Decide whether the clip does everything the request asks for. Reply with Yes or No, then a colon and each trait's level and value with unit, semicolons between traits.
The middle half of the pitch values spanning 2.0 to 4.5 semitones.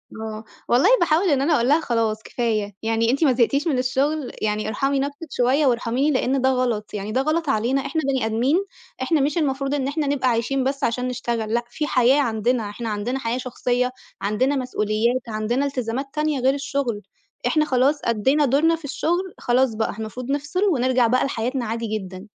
Yes: average, 3.6 semitones